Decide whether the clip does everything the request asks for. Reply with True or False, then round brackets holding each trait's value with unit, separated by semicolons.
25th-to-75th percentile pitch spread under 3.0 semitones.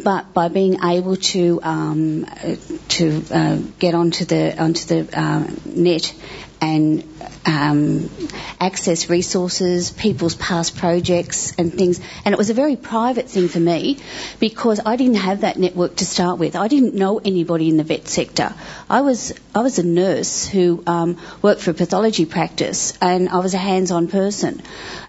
True (2.5 semitones)